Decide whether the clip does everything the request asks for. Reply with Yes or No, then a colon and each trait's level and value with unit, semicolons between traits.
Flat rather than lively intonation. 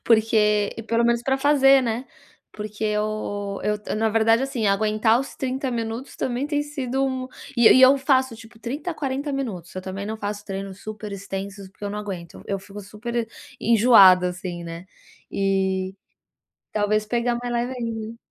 No: average, 3.7 semitones